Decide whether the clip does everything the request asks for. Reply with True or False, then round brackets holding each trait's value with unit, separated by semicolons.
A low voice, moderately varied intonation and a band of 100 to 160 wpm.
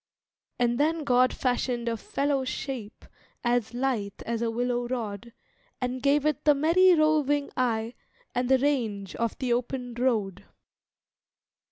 False (250 Hz; 3.0 semitones; 140 wpm)